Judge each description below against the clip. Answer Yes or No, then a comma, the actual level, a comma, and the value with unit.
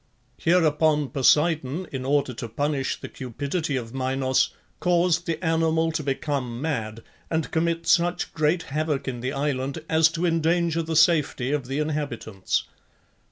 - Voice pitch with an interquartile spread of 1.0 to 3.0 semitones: No, average, 3.5 semitones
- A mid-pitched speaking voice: Yes, medium, 150 Hz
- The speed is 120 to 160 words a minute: Yes, average, 145 wpm